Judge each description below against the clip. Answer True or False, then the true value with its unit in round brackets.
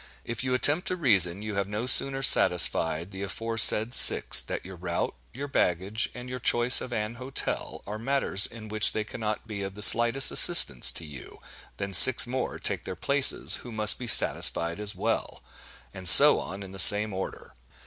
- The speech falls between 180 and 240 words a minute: True (190 wpm)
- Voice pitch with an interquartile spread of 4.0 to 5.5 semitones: True (4.3 semitones)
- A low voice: True (110 Hz)